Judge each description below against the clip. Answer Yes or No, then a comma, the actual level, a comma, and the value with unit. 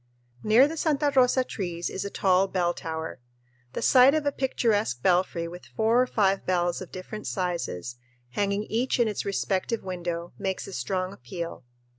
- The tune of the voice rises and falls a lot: No, average, 4.6 semitones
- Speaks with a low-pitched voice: No, high, 190 Hz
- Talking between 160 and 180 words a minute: Yes, average, 170 wpm